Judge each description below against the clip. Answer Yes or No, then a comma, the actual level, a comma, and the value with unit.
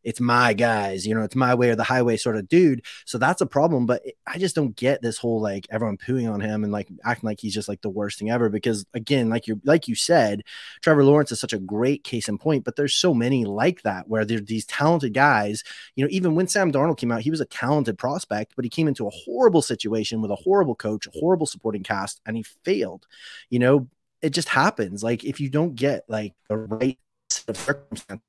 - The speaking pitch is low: Yes, low, 120 Hz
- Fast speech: Yes, fast, 245 wpm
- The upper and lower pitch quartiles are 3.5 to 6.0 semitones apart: Yes, average, 4.7 semitones